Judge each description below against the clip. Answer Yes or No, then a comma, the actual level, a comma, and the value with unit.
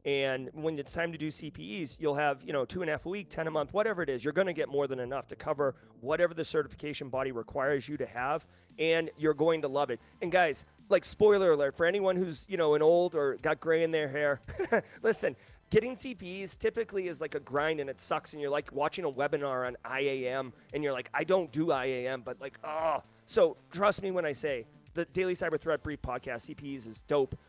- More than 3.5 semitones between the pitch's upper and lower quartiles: Yes, average, 4.4 semitones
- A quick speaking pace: Yes, fast, 235 wpm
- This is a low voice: No, medium, 155 Hz